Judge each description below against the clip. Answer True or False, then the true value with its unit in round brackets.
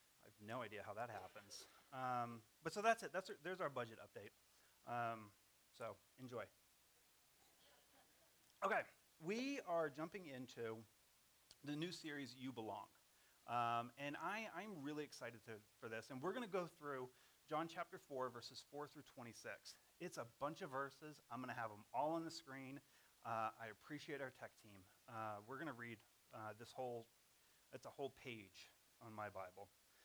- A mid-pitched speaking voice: False (130 Hz)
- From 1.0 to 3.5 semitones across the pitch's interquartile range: False (4.7 semitones)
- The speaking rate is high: False (175 wpm)